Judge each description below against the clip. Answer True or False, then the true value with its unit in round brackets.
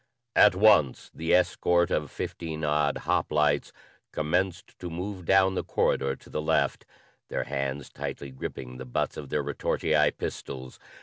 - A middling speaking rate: True (145 wpm)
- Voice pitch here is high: False (75 Hz)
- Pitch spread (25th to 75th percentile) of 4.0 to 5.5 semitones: True (4.4 semitones)